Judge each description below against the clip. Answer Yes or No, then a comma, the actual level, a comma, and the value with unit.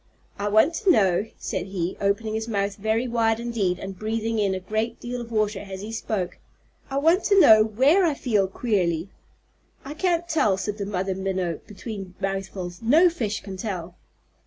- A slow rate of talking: No, average, 185 wpm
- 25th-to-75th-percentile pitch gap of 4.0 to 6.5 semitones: No, average, 3.5 semitones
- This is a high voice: Yes, high, 215 Hz